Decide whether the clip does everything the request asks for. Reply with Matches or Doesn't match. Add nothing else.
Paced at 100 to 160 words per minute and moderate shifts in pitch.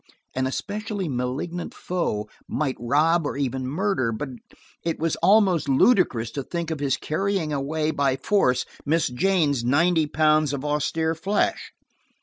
Matches